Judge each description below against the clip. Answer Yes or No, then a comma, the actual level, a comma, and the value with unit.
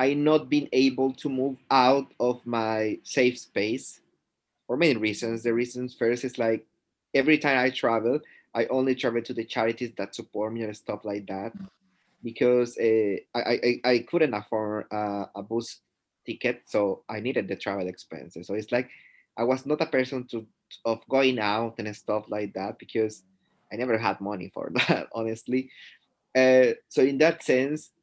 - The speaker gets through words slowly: No, average, 175 wpm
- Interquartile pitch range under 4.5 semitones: Yes, average, 3.4 semitones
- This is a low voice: Yes, low, 115 Hz